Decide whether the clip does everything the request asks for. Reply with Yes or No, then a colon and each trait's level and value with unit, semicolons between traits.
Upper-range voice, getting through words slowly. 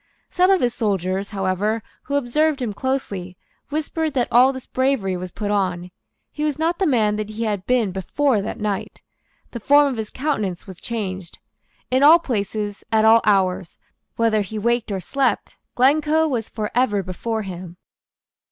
No: high, 220 Hz; average, 170 wpm